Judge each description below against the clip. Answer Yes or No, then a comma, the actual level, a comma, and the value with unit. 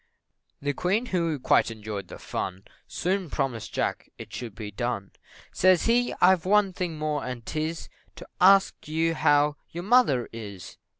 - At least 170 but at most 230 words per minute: No, average, 160 wpm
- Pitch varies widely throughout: Yes, wide, 7.8 semitones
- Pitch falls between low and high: Yes, medium, 155 Hz